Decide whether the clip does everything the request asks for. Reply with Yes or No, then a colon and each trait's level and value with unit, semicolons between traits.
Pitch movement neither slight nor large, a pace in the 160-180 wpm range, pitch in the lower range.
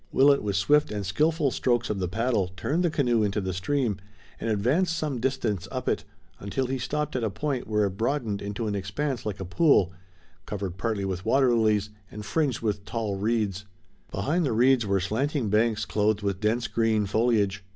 No: average, 4.8 semitones; average, 195 wpm; low, 110 Hz